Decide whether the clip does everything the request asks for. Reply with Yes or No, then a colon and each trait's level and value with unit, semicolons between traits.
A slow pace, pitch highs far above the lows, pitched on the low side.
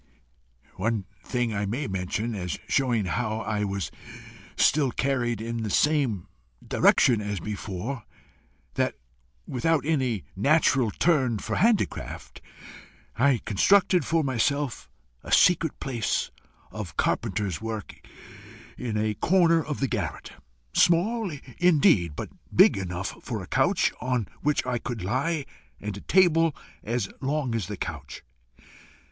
Yes: slow, 130 wpm; wide, 6.0 semitones; low, 120 Hz